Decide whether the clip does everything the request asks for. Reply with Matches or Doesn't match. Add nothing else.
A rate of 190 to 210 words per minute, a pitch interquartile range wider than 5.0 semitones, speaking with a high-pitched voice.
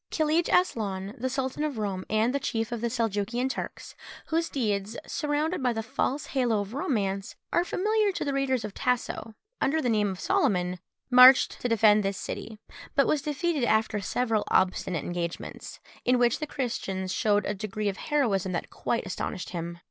Doesn't match